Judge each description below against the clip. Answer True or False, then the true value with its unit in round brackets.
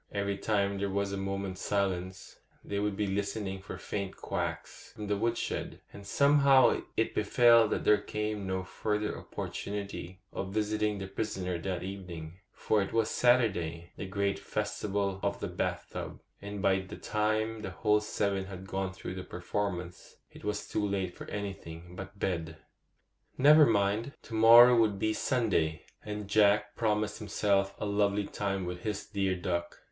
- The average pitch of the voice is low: True (100 Hz)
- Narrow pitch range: True (1.9 semitones)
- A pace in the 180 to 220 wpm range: False (160 wpm)